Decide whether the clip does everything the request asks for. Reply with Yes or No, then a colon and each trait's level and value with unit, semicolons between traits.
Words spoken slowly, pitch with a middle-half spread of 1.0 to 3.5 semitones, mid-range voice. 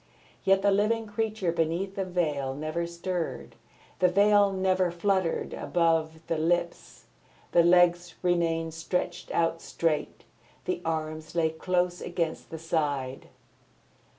Yes: slow, 125 wpm; narrow, 2.4 semitones; medium, 170 Hz